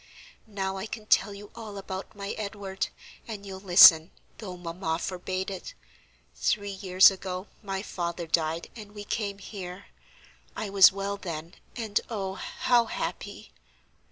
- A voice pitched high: Yes, high, 195 Hz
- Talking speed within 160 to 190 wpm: No, average, 145 wpm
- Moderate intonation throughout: No, narrow, 1.9 semitones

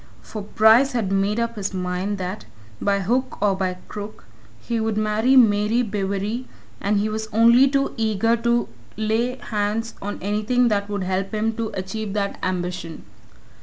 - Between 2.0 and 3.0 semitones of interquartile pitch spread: Yes, narrow, 2.5 semitones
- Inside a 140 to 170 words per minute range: Yes, average, 165 wpm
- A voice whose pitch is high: Yes, high, 210 Hz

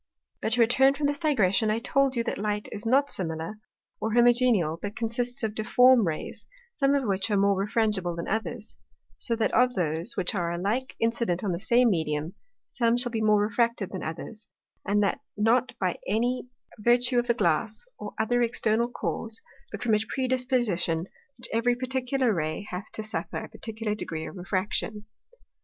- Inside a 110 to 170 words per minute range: No, average, 180 wpm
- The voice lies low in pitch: No, high, 220 Hz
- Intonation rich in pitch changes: No, average, 3.7 semitones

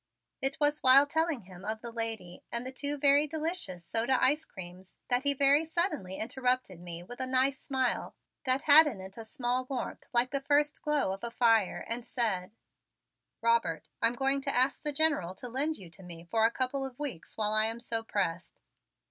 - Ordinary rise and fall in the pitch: Yes, average, 4.7 semitones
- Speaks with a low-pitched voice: No, high, 245 Hz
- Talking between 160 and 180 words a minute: No, average, 200 wpm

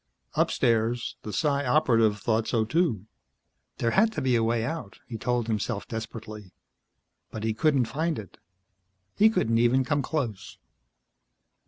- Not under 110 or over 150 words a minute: Yes, average, 145 wpm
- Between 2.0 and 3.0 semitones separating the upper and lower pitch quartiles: No, average, 4.2 semitones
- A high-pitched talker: No, low, 115 Hz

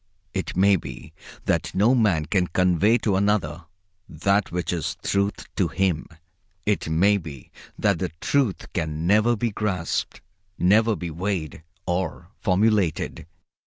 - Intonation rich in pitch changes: No, average, 3.7 semitones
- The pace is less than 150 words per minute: Yes, average, 140 wpm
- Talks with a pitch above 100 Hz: No, very low, 95 Hz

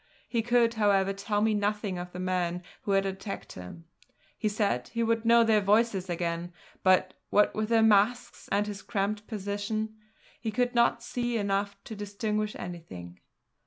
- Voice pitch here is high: Yes, high, 205 Hz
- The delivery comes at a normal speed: Yes, average, 165 wpm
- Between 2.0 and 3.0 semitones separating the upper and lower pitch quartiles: Yes, narrow, 2.6 semitones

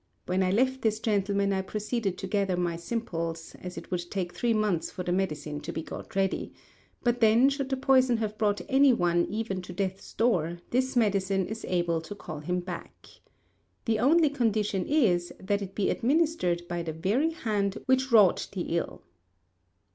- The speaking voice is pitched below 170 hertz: No, high, 200 Hz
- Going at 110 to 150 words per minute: No, average, 180 wpm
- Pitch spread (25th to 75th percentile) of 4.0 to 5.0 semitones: Yes, average, 4.7 semitones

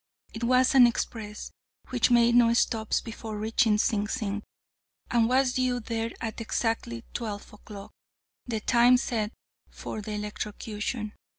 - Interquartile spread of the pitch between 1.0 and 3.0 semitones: Yes, narrow, 2.4 semitones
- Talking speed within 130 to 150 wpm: Yes, slow, 135 wpm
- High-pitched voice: Yes, high, 225 Hz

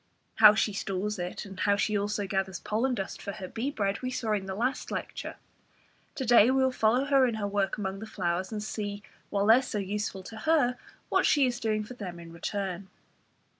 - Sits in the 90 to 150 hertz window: No, high, 210 Hz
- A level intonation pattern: No, average, 3.4 semitones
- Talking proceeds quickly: Yes, fast, 220 wpm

